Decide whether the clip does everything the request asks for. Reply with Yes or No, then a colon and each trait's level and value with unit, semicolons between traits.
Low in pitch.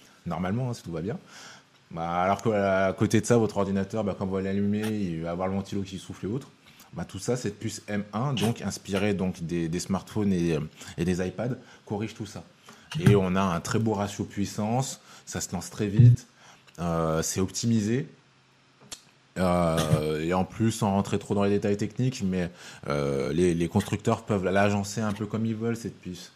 Yes: low, 100 Hz